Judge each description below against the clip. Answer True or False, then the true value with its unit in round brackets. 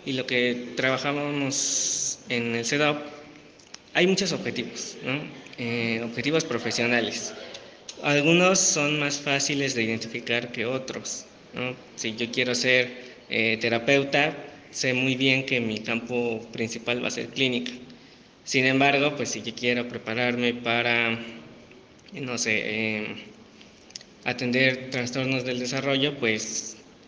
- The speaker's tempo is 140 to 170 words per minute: False (125 wpm)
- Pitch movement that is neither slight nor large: True (3.0 semitones)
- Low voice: True (125 Hz)